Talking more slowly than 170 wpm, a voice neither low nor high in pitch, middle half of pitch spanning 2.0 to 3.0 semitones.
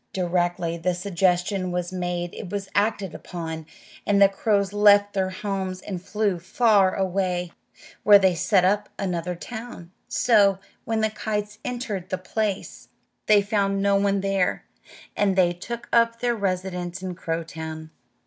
No: average, 150 wpm; high, 195 Hz; narrow, 2.5 semitones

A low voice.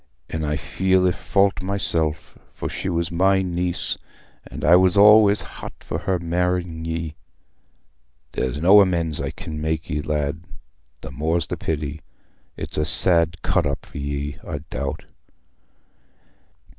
Yes: very low, 85 Hz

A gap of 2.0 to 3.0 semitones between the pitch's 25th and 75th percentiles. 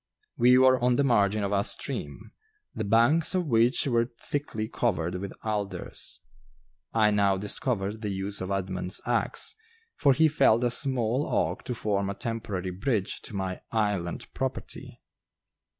No: average, 3.9 semitones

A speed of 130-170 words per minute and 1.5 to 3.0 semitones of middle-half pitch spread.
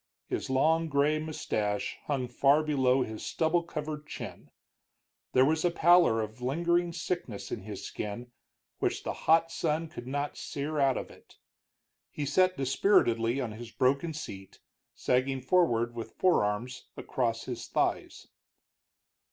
No: average, 145 wpm; average, 5.0 semitones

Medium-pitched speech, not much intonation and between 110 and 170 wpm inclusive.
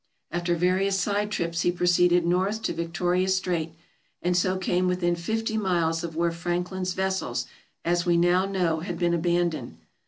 Yes: medium, 175 Hz; narrow, 1.6 semitones; average, 160 wpm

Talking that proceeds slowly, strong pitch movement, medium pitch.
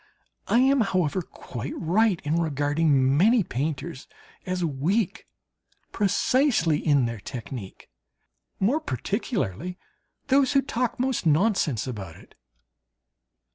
Yes: slow, 105 wpm; wide, 8.2 semitones; medium, 170 Hz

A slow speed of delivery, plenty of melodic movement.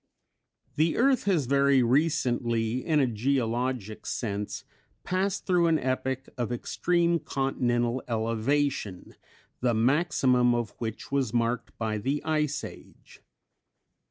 No: slow, 115 wpm; average, 4.2 semitones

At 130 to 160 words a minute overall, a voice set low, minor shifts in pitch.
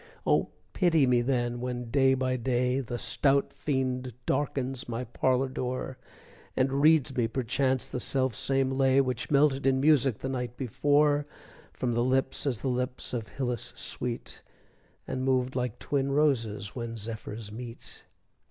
Yes: average, 150 wpm; low, 130 Hz; narrow, 1.9 semitones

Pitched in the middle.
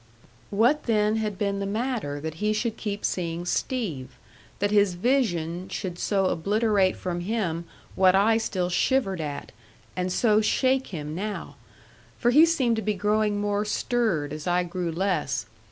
No: high, 200 Hz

